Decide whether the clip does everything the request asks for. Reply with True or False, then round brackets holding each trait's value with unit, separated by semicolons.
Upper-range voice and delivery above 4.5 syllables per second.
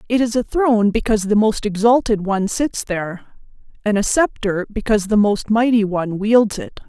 True (215 Hz; 5.4 syllables/s)